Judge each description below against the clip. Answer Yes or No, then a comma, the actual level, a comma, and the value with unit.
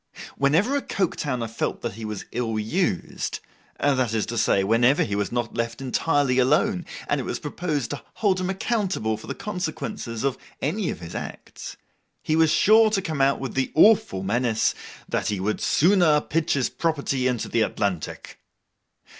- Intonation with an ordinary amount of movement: No, wide, 7.0 semitones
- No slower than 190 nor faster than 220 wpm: No, average, 165 wpm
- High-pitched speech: No, low, 135 Hz